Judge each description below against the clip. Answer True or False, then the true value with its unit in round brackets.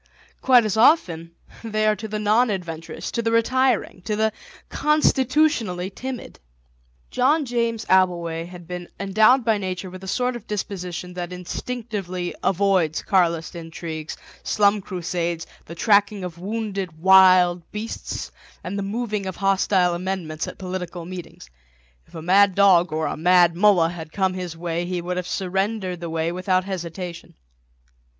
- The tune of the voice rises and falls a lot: False (3.5 semitones)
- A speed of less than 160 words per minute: True (150 wpm)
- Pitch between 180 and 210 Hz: True (185 Hz)